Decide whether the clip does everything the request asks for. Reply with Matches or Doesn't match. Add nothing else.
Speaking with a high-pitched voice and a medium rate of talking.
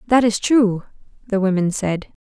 Matches